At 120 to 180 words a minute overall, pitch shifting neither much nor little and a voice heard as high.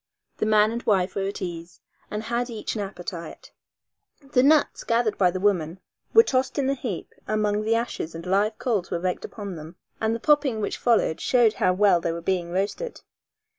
No: average, 200 wpm; average, 4.4 semitones; high, 210 Hz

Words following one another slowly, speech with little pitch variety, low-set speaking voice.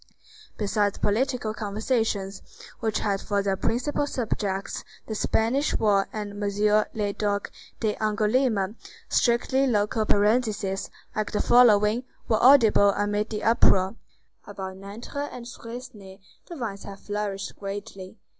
No: slow, 120 wpm; narrow, 2.3 semitones; high, 210 Hz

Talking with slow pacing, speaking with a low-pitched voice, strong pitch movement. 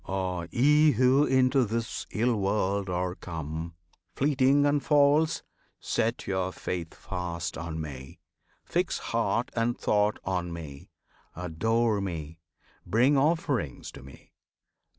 Yes: slow, 120 wpm; low, 100 Hz; wide, 7.2 semitones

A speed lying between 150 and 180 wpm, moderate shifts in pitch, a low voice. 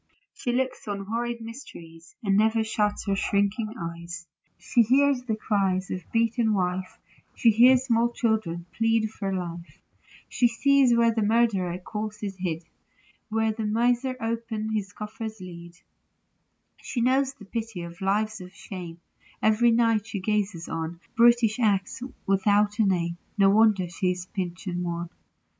No: average, 155 wpm; average, 3.7 semitones; high, 210 Hz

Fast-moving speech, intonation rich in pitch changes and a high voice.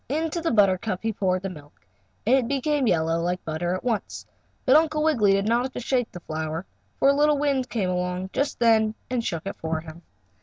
Yes: fast, 220 wpm; wide, 6.8 semitones; high, 215 Hz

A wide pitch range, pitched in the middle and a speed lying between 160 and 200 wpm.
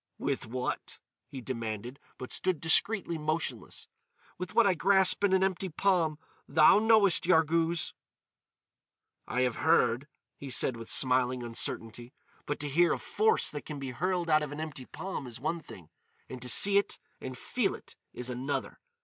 Yes: wide, 6.2 semitones; medium, 150 Hz; average, 165 wpm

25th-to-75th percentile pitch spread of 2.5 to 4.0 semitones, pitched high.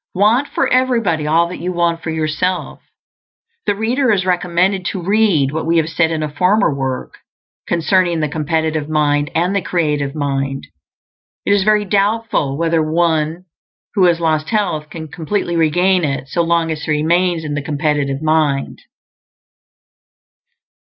No: average, 3.3 semitones; medium, 165 Hz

